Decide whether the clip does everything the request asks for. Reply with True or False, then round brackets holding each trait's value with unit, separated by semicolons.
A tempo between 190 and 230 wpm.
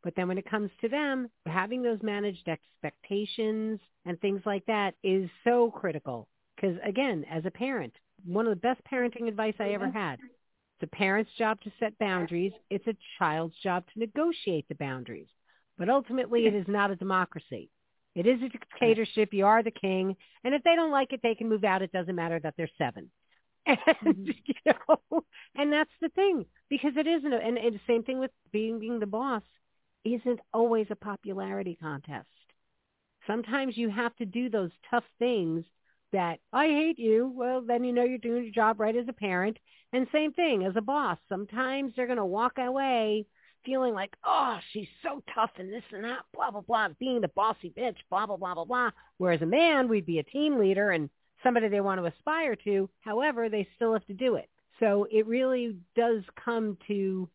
True (195 wpm)